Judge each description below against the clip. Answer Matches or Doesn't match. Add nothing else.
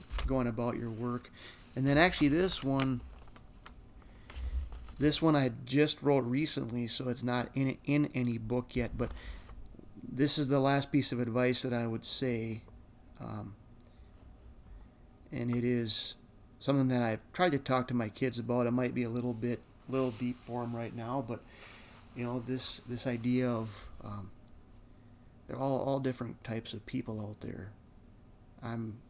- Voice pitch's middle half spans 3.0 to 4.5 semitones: Doesn't match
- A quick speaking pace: Doesn't match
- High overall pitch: Doesn't match